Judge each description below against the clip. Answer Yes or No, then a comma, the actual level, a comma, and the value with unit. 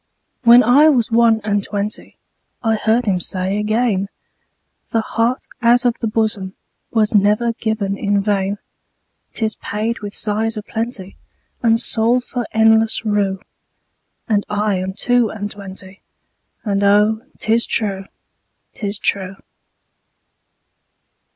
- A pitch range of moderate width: No, narrow, 2.1 semitones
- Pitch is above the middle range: Yes, high, 215 Hz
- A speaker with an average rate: No, slow, 105 wpm